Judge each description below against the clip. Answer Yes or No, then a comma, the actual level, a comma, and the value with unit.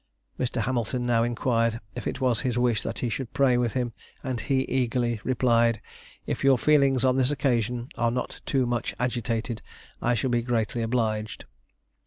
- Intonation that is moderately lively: No, narrow, 1.8 semitones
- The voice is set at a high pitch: No, low, 120 Hz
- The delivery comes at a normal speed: Yes, average, 175 wpm